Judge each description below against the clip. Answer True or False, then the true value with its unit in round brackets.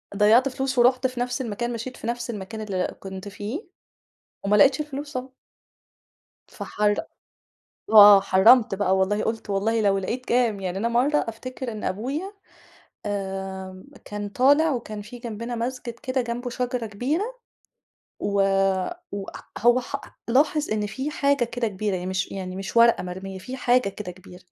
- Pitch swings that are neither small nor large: True (4.2 semitones)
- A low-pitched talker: False (225 Hz)